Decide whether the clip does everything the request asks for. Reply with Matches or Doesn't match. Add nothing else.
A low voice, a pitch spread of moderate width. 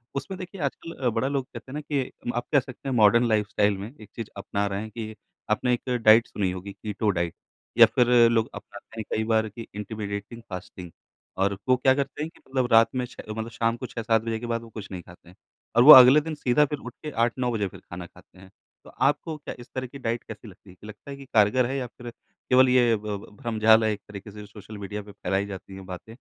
Matches